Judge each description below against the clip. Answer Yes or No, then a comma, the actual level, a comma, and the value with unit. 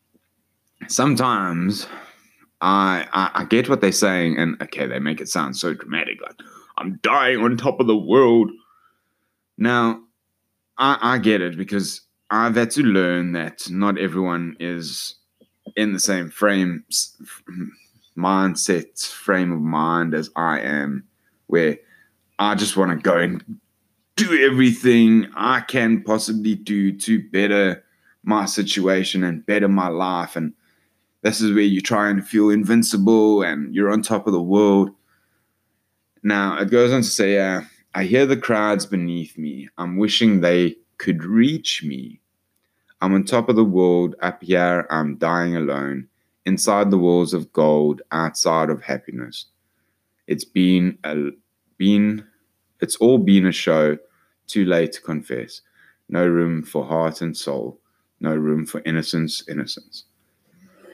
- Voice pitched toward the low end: Yes, low, 100 Hz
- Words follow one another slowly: No, average, 145 wpm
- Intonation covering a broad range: No, average, 3.8 semitones